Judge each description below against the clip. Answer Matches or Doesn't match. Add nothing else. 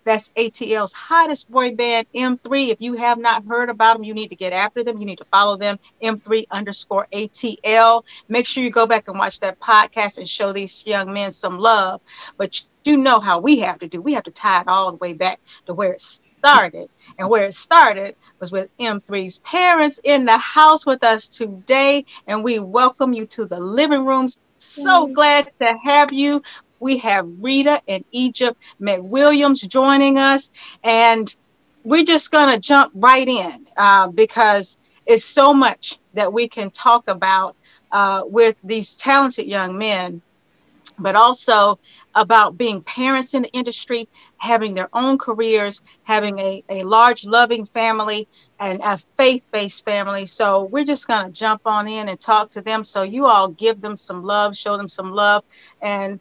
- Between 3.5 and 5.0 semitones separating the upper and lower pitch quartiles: Matches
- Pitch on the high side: Matches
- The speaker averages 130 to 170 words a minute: Doesn't match